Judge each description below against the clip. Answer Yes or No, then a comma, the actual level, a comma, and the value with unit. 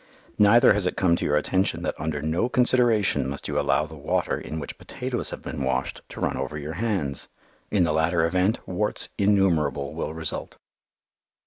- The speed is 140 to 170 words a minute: No, average, 185 wpm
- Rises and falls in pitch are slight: No, average, 5.1 semitones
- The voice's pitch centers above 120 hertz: No, very low, 85 Hz